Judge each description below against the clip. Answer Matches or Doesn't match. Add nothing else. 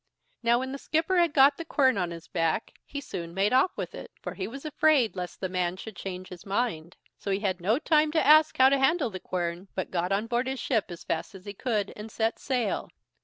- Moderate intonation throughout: Doesn't match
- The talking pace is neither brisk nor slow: Doesn't match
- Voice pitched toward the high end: Matches